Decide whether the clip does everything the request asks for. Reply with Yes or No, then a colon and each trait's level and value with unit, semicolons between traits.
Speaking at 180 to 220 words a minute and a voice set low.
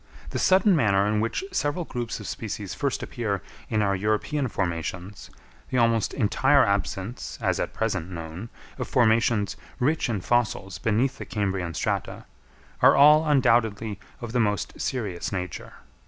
No: average, 150 wpm; low, 110 Hz